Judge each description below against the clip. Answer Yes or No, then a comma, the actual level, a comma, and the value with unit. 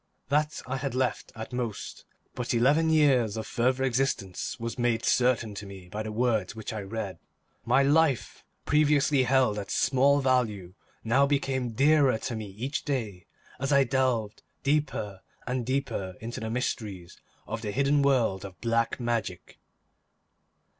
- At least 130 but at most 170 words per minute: Yes, average, 155 wpm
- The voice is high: No, low, 120 Hz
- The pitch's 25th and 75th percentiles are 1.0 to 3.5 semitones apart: No, average, 3.9 semitones